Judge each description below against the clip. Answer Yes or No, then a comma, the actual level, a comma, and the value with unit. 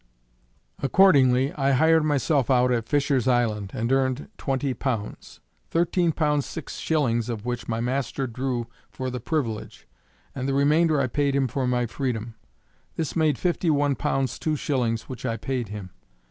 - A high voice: No, low, 130 Hz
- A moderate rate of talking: Yes, average, 160 wpm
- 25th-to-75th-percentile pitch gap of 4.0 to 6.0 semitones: No, average, 3.1 semitones